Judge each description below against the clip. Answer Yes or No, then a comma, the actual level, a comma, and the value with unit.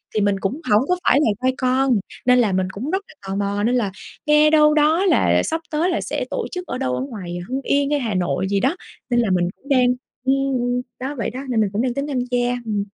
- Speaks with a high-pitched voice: Yes, very high, 250 Hz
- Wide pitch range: Yes, wide, 6.0 semitones